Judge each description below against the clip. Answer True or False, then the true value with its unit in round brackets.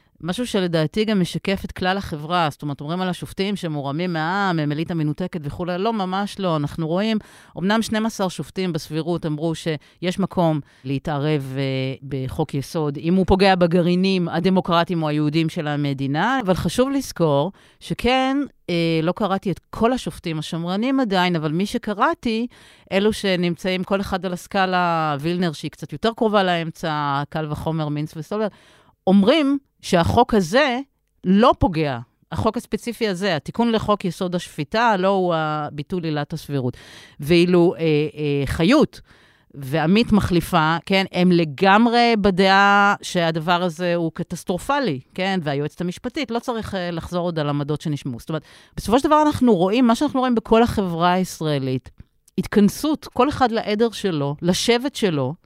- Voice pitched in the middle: True (180 Hz)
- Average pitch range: True (4.7 semitones)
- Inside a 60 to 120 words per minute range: False (145 wpm)